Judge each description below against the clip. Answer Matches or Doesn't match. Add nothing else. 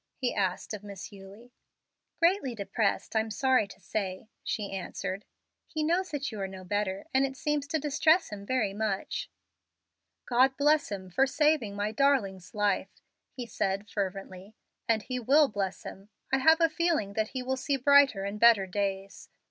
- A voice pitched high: Matches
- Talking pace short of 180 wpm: Matches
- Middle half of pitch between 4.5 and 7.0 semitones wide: Matches